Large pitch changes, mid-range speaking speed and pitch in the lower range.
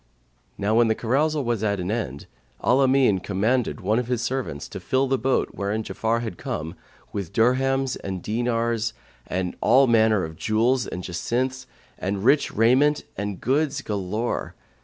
No: average, 4.3 semitones; average, 160 wpm; low, 115 Hz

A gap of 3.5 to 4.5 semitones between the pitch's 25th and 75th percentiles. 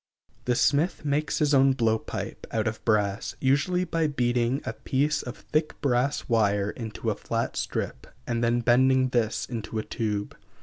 Yes: average, 4.0 semitones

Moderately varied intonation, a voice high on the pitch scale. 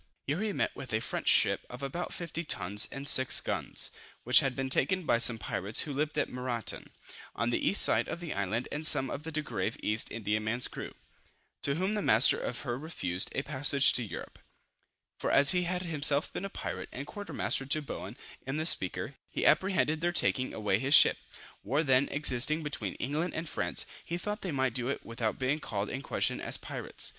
No: average, 5.0 semitones; low, 135 Hz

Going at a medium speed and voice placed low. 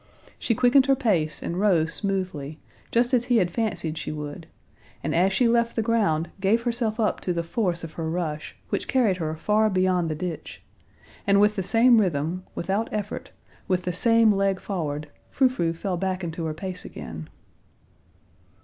No: average, 180 wpm; high, 190 Hz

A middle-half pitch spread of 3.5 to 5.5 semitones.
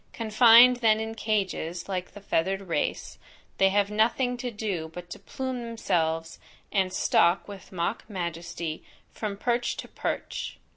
Yes: average, 4.3 semitones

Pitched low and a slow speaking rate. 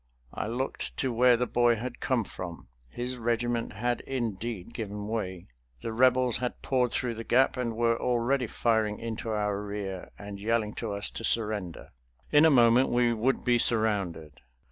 No: low, 115 Hz; average, 170 wpm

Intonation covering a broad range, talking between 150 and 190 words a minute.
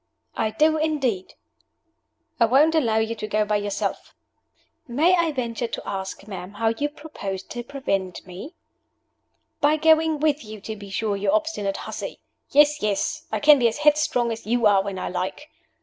Yes: wide, 6.6 semitones; average, 175 wpm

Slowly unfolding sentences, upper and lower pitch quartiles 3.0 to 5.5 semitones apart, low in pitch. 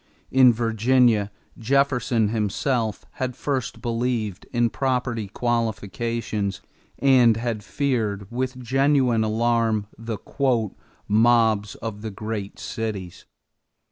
No: slow, 95 wpm; narrow, 2.6 semitones; low, 115 Hz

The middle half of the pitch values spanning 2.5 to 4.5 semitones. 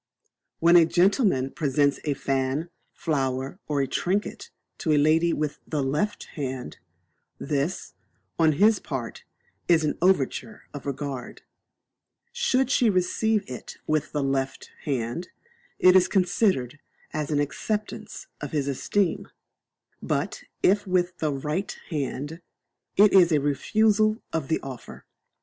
No: average, 5.1 semitones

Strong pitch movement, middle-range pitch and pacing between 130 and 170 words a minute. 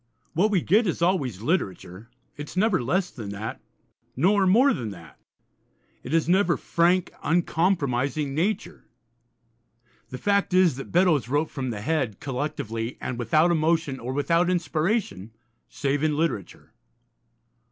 Yes: wide, 6.2 semitones; medium, 155 Hz; average, 140 wpm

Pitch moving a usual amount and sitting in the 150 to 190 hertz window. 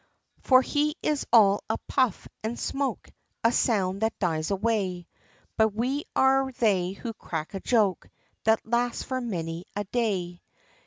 No: average, 4.5 semitones; high, 220 Hz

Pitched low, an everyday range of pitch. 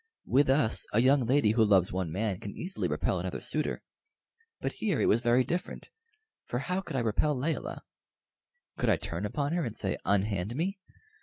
No: low, 125 Hz; wide, 6.1 semitones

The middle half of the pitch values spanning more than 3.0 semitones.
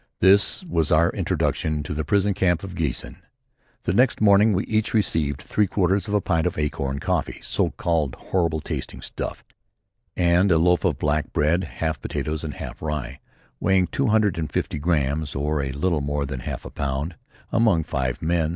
Yes: average, 4.2 semitones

